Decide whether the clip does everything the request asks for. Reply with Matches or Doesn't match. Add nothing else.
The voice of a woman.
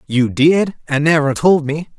Doesn't match